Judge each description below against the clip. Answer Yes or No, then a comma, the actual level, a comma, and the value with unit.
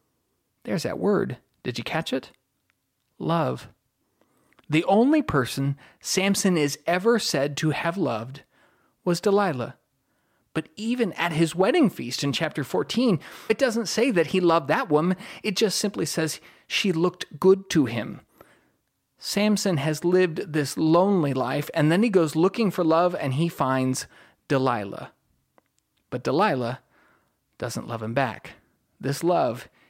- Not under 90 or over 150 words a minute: Yes, average, 140 wpm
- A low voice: No, medium, 170 Hz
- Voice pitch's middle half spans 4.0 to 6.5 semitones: Yes, average, 5.0 semitones